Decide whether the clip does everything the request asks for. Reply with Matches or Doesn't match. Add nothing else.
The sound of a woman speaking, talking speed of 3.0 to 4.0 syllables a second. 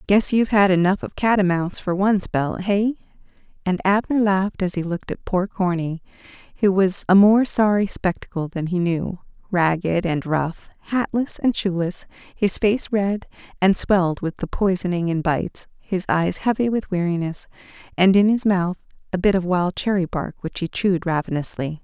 Doesn't match